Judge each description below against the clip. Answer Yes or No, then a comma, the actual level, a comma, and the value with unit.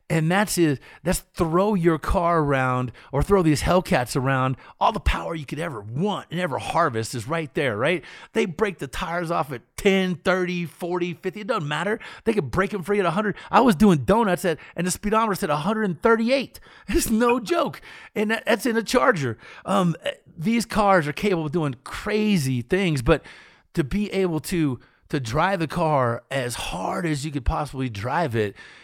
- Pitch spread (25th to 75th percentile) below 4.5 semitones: No, average, 5.3 semitones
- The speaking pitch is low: No, medium, 175 Hz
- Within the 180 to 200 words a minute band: Yes, average, 190 wpm